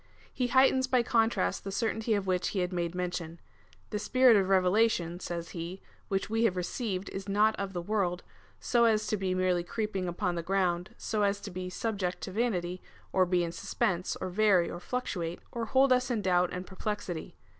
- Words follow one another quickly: Yes, fast, 210 wpm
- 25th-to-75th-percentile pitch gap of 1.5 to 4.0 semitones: Yes, average, 3.6 semitones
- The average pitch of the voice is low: No, high, 190 Hz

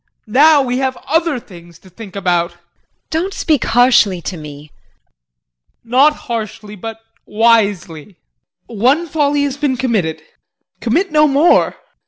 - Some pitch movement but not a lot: No, wide, 6.8 semitones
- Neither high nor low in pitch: No, high, 235 Hz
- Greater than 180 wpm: No, slow, 135 wpm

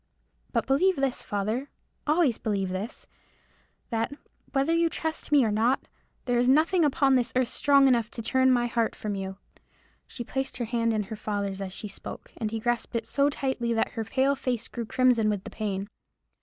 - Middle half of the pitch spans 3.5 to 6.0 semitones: Yes, average, 4.0 semitones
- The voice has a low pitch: No, high, 240 Hz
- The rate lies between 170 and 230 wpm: Yes, average, 185 wpm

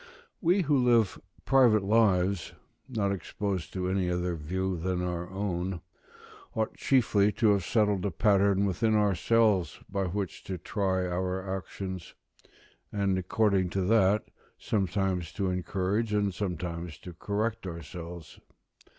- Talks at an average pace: No, slow, 130 wpm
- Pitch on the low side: Yes, very low, 95 Hz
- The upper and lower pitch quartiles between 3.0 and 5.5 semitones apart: No, narrow, 2.6 semitones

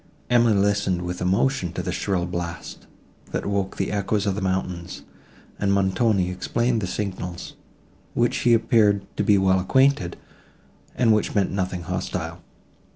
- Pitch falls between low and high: No, very low, 95 Hz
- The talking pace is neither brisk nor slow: Yes, average, 155 wpm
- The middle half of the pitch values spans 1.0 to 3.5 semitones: Yes, average, 2.7 semitones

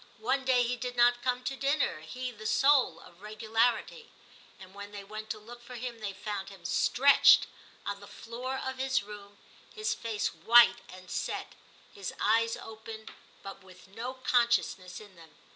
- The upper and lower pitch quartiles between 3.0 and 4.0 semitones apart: Yes, average, 3.7 semitones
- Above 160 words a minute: Yes, average, 175 wpm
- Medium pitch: No, high, 225 Hz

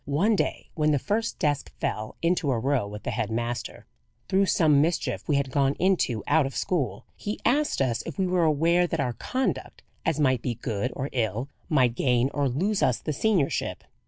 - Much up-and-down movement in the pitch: Yes, wide, 5.7 semitones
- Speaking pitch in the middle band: Yes, medium, 145 Hz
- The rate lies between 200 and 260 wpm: Yes, fast, 205 wpm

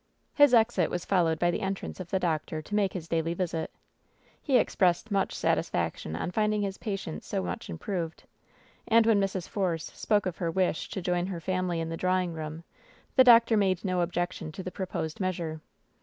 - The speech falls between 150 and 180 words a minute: No, average, 195 wpm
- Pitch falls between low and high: Yes, medium, 180 Hz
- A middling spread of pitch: Yes, average, 3.1 semitones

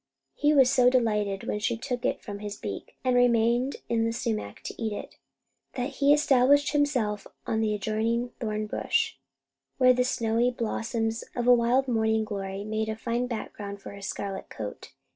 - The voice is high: Yes, high, 230 Hz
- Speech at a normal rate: Yes, average, 180 wpm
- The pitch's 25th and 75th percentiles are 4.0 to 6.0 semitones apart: No, average, 2.8 semitones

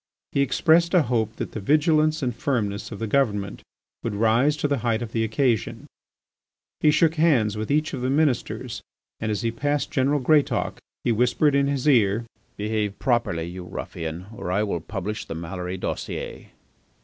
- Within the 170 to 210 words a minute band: Yes, average, 175 wpm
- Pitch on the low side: Yes, low, 115 Hz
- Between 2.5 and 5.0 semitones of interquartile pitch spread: No, wide, 5.4 semitones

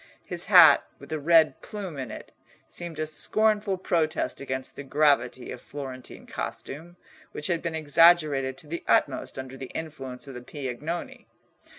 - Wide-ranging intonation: No, average, 4.2 semitones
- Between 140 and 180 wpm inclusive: Yes, average, 160 wpm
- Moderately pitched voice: Yes, medium, 155 Hz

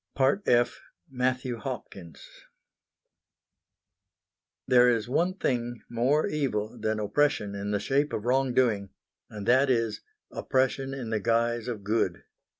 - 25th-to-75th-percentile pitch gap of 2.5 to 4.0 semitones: Yes, average, 3.4 semitones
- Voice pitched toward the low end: Yes, low, 120 Hz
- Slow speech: Yes, slow, 125 wpm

